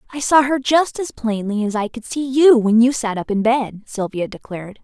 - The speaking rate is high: Yes, fast, 235 wpm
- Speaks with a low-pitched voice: No, high, 240 Hz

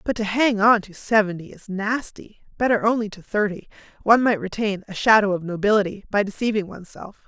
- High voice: Yes, high, 205 Hz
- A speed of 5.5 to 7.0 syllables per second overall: Yes, 5.9 syllables/s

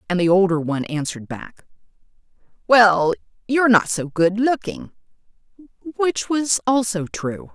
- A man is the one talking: No, female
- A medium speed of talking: No, slow, 125 wpm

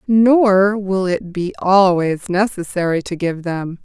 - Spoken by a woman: Yes, female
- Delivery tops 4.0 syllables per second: No, 3.6 syllables/s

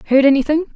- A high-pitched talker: Yes, very high, 285 Hz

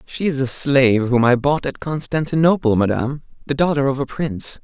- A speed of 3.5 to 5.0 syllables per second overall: No, 5.6 syllables/s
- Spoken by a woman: No, male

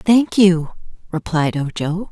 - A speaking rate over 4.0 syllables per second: No, 3.6 syllables/s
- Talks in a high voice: No, medium, 180 Hz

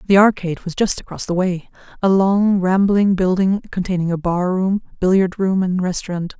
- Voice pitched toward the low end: No, medium, 185 Hz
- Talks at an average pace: Yes, average, 160 wpm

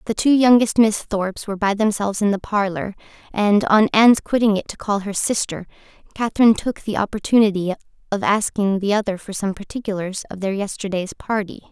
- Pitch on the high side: Yes, high, 205 Hz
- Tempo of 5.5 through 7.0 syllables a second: Yes, 5.8 syllables/s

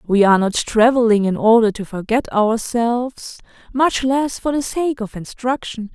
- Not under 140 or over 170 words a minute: Yes, average, 160 wpm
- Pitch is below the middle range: No, high, 230 Hz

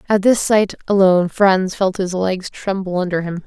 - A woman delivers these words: Yes, female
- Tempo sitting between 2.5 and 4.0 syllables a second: No, 4.7 syllables/s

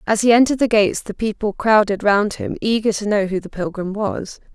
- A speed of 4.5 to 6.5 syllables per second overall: Yes, 5.7 syllables/s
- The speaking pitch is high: Yes, high, 205 Hz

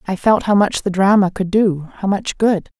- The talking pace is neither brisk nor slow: No, fast, 215 wpm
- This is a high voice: Yes, high, 195 Hz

